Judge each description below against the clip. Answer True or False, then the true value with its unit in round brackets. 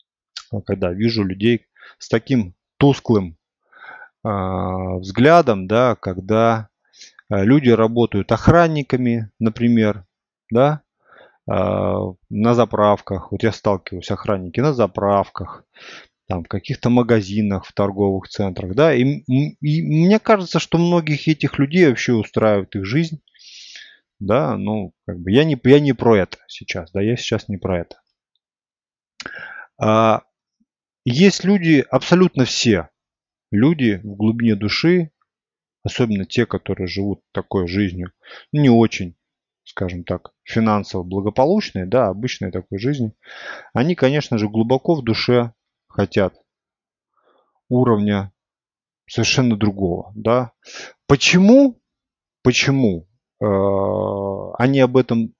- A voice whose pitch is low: True (115 Hz)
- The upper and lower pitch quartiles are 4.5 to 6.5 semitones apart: True (4.8 semitones)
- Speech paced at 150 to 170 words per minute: False (110 wpm)